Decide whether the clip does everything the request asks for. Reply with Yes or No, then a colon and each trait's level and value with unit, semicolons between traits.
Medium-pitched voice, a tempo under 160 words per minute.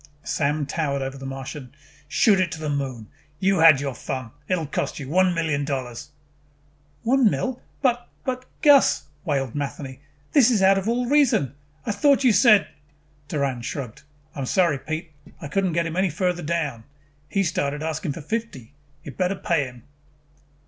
No: medium, 155 Hz; average, 175 wpm